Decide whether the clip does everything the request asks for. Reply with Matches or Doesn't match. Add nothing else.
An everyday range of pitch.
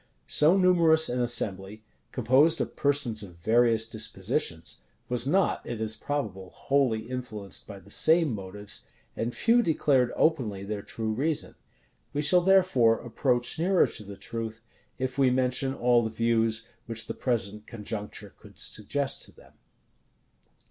Matches